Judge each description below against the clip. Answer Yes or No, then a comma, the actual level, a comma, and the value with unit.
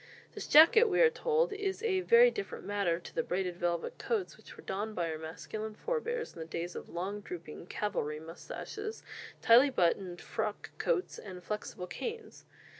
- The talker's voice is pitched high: Yes, high, 215 Hz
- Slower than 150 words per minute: No, average, 175 wpm